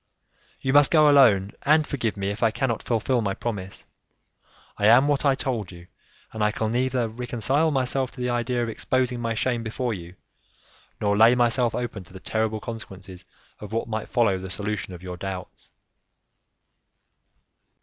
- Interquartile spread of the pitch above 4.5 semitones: No, average, 3.7 semitones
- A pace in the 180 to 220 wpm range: No, average, 170 wpm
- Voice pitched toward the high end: No, low, 115 Hz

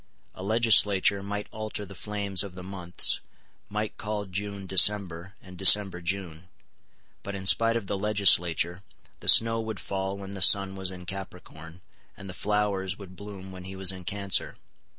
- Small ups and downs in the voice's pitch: Yes, narrow, 1.8 semitones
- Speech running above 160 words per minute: Yes, average, 170 wpm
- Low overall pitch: Yes, very low, 95 Hz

